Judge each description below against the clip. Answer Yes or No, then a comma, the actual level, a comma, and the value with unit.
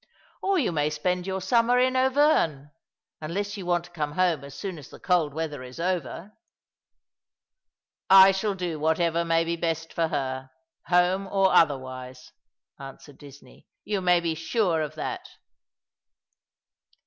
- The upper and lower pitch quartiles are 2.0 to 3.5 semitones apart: No, average, 4.2 semitones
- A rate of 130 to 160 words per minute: No, average, 170 wpm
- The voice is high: No, medium, 170 Hz